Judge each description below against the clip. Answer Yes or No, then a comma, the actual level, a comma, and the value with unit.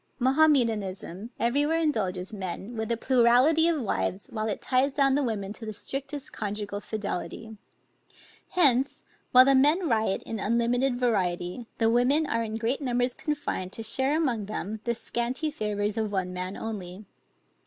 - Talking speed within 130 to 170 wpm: Yes, average, 160 wpm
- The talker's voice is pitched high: Yes, high, 230 Hz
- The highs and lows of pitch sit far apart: No, average, 4.5 semitones